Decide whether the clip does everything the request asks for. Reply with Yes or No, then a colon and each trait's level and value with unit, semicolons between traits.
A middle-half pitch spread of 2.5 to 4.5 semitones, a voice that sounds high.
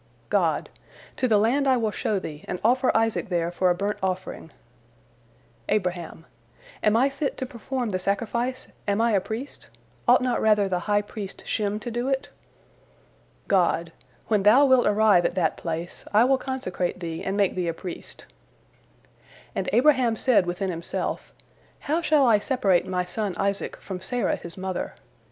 No: average, 5.0 semitones; high, 210 Hz